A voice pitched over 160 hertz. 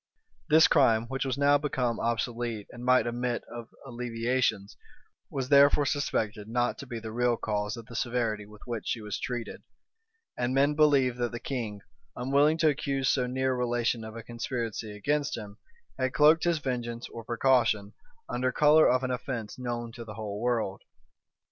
No: low, 120 Hz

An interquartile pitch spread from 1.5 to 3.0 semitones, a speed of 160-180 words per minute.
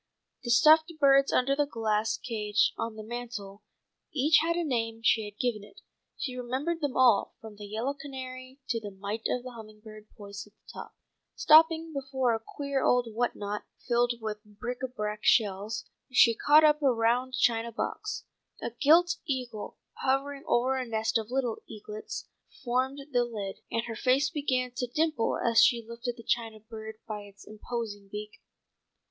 No: average, 3.5 semitones; average, 175 wpm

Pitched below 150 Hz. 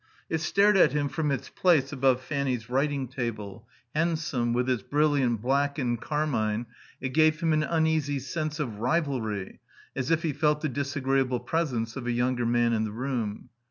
Yes: low, 135 Hz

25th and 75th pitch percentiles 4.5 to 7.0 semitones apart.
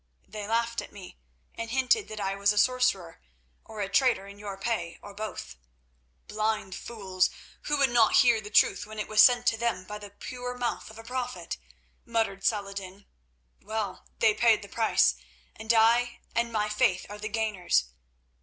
No: average, 2.8 semitones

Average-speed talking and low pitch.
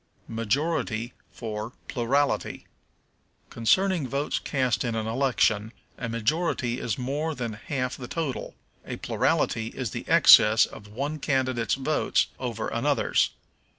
No: slow, 120 wpm; low, 125 Hz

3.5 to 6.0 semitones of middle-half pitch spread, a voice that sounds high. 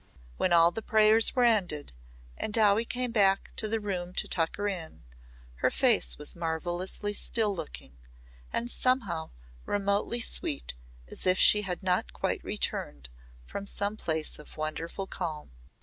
Yes: average, 4.7 semitones; high, 195 Hz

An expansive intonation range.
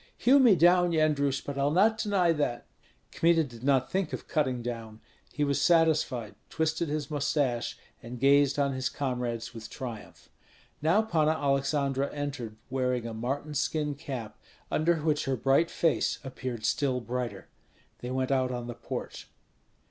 No: average, 3.8 semitones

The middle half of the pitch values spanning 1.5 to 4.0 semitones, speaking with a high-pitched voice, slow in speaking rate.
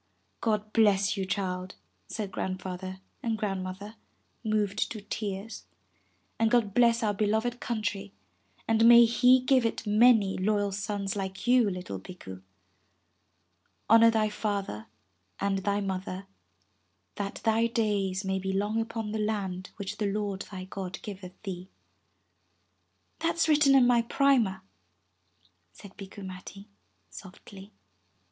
Yes: average, 2.8 semitones; high, 205 Hz; slow, 130 wpm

